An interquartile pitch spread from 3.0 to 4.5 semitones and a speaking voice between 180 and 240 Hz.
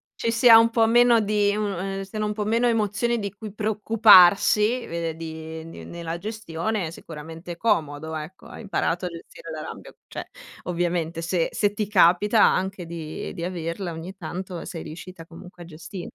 Yes: average, 4.1 semitones; medium, 185 Hz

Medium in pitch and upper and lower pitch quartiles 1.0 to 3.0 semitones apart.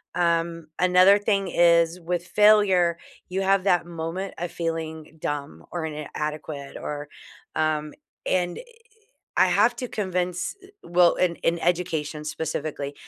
Yes: medium, 170 Hz; narrow, 2.5 semitones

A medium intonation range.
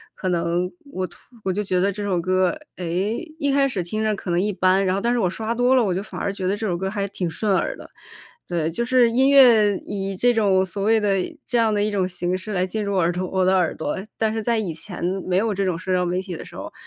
Yes: average, 3.0 semitones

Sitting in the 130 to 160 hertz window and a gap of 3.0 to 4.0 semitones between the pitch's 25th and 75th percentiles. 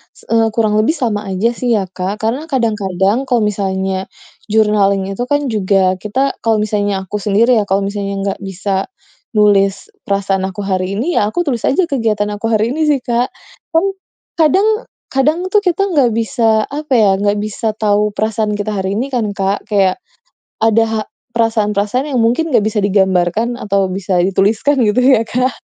No: high, 215 Hz; average, 3.3 semitones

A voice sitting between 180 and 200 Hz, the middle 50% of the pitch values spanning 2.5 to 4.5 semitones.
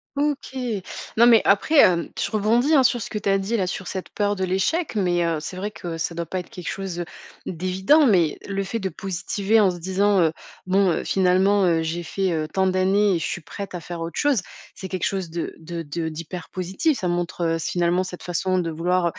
Yes: medium, 185 Hz; average, 2.8 semitones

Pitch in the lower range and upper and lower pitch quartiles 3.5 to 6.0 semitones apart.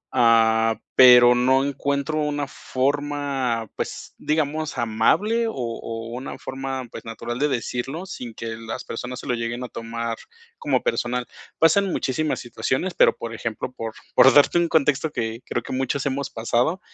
Yes: low, 130 Hz; average, 3.8 semitones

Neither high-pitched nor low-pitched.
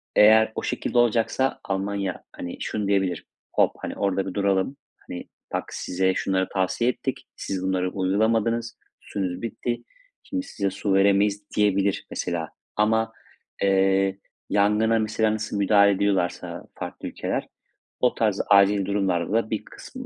No: low, 100 Hz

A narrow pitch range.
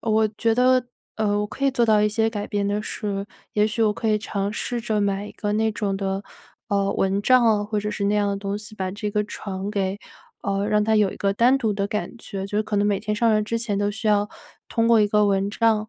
Yes: narrow, 1.5 semitones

